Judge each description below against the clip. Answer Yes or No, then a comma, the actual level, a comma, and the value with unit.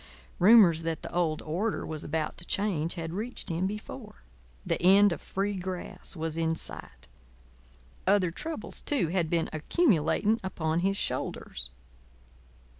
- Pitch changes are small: No, average, 3.8 semitones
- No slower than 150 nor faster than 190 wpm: No, average, 140 wpm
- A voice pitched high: No, medium, 175 Hz